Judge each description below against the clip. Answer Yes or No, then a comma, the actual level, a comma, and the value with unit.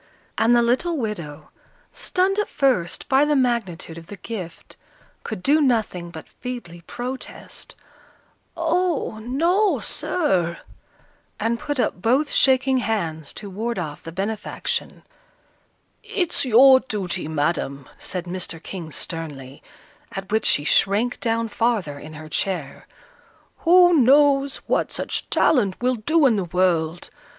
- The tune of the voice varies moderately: No, wide, 7.5 semitones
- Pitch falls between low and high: No, high, 220 Hz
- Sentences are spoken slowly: Yes, slow, 130 wpm